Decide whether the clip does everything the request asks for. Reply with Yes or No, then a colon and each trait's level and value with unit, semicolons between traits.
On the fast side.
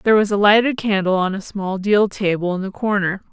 Yes: fast, 235 wpm